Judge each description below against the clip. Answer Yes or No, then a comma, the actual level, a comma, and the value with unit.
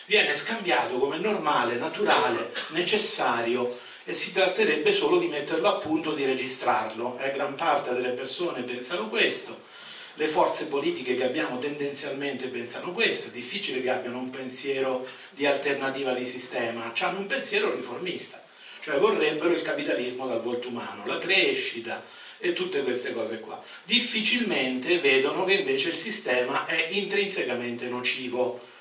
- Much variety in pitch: Yes, wide, 8.4 semitones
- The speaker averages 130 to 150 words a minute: Yes, average, 140 wpm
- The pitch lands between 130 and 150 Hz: Yes, medium, 140 Hz